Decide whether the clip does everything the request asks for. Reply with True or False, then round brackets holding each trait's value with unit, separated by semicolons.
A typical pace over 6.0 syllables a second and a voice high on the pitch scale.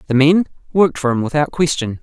False (6.3 syllables/s; 145 Hz)